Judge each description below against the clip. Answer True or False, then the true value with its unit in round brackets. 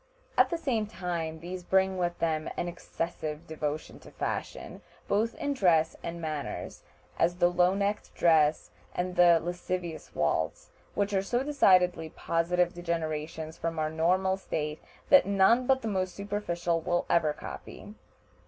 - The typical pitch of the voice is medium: True (175 Hz)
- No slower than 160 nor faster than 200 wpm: False (150 wpm)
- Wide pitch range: False (3.1 semitones)